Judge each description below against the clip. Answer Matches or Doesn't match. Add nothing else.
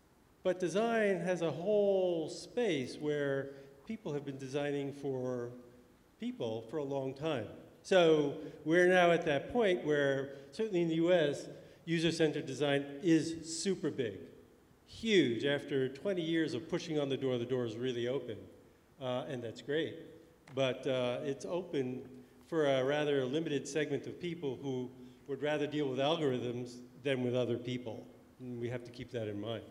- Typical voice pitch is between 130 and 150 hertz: Matches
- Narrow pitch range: Doesn't match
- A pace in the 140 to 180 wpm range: Matches